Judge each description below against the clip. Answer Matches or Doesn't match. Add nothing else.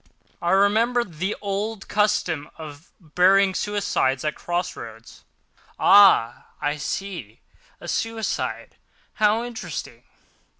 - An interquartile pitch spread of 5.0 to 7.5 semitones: Matches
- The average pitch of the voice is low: Doesn't match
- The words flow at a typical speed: Doesn't match